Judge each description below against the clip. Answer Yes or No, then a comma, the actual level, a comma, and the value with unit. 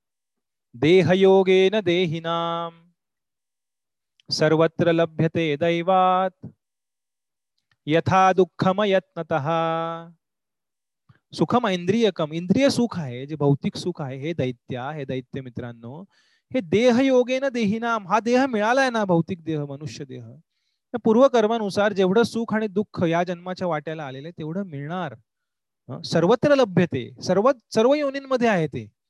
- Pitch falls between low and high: Yes, medium, 180 Hz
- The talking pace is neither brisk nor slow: Yes, average, 100 wpm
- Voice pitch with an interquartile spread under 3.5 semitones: No, average, 5.1 semitones